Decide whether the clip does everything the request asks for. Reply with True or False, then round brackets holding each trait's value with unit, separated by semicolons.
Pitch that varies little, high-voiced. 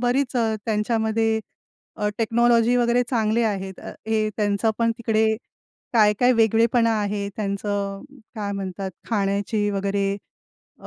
True (2.3 semitones; 215 Hz)